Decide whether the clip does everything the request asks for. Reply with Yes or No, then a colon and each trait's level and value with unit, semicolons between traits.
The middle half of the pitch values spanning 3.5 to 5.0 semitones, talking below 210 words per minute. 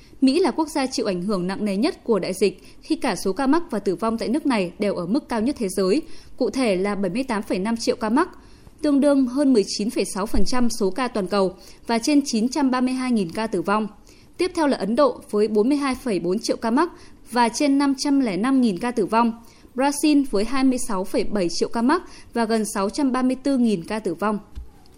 No: wide, 5.4 semitones; average, 190 wpm